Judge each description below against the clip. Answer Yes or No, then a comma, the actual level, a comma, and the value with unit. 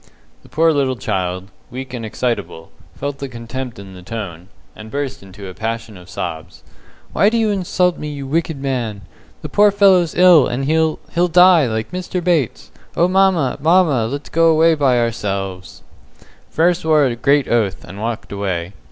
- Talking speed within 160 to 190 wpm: Yes, average, 175 wpm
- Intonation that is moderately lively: No, wide, 7.3 semitones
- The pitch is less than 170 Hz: Yes, low, 135 Hz